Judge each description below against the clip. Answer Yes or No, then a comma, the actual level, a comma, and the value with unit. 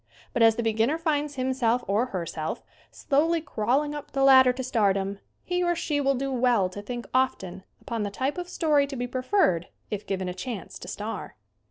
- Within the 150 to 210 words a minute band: Yes, average, 200 wpm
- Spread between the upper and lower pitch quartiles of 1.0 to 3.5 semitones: No, average, 5.3 semitones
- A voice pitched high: Yes, very high, 250 Hz